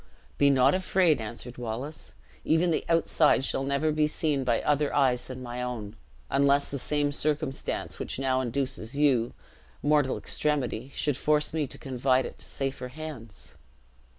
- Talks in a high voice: No, medium, 140 Hz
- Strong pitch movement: No, average, 2.9 semitones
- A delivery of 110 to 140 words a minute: No, average, 155 wpm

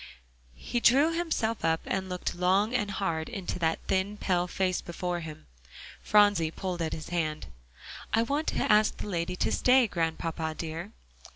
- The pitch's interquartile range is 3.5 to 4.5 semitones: Yes, average, 4.2 semitones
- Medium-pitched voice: Yes, medium, 180 Hz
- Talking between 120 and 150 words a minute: No, average, 165 wpm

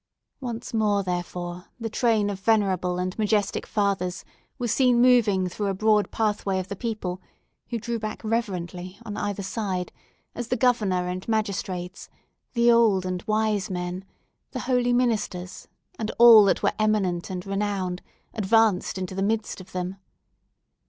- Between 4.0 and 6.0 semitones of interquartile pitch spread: No, average, 3.4 semitones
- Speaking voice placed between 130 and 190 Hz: No, high, 205 Hz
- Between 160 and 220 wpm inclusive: No, average, 150 wpm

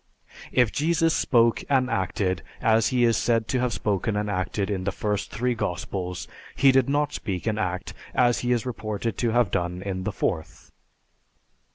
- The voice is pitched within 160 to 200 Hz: No, low, 110 Hz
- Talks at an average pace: Yes, average, 180 wpm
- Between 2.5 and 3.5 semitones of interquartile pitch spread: No, average, 4.3 semitones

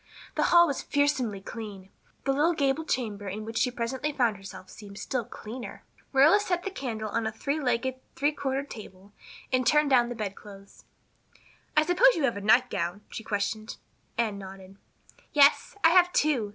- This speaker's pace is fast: No, average, 175 wpm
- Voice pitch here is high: Yes, high, 240 Hz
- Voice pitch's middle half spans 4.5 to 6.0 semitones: Yes, wide, 5.6 semitones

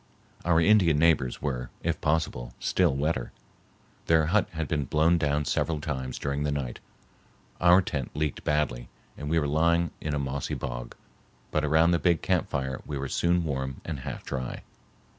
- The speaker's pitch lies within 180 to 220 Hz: No, very low, 75 Hz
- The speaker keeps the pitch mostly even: No, average, 3.4 semitones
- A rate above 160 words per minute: Yes, average, 175 wpm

